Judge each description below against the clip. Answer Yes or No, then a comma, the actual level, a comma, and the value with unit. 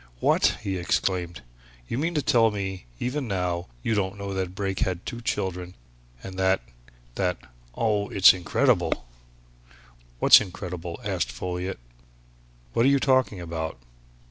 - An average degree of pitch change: Yes, average, 3.2 semitones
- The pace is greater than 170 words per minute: No, average, 145 wpm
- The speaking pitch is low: Yes, very low, 95 Hz